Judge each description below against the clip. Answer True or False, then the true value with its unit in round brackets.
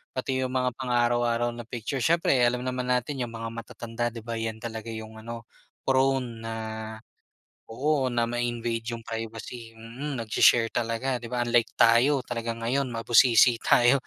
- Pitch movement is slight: True (1.7 semitones)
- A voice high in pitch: False (120 Hz)